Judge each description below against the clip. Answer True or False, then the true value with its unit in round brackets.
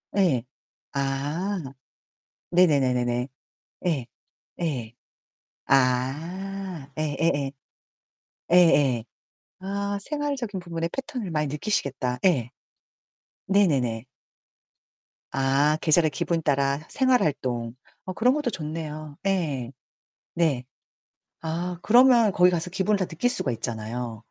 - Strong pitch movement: True (6.0 semitones)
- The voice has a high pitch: False (160 Hz)